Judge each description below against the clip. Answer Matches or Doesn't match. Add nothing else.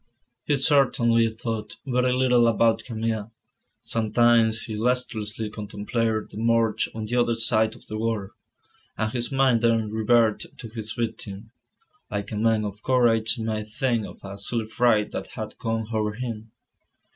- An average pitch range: Doesn't match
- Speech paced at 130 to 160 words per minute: Matches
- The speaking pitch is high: Doesn't match